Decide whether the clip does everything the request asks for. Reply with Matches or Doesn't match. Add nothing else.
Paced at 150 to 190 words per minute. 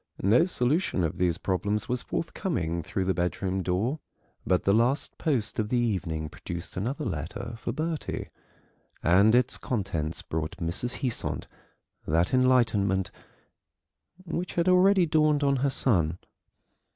Doesn't match